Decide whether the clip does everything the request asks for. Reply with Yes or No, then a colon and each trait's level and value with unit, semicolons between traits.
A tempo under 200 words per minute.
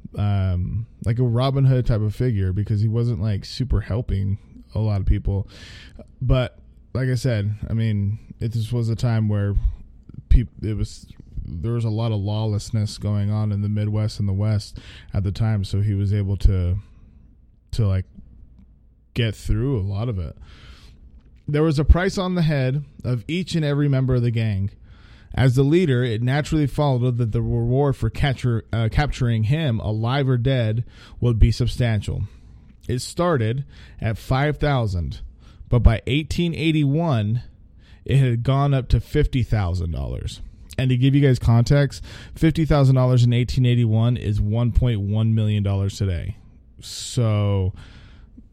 Yes: average, 165 wpm